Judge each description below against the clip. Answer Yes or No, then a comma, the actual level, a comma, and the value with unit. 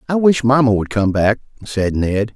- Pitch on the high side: No, low, 115 Hz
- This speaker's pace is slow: No, fast, 205 wpm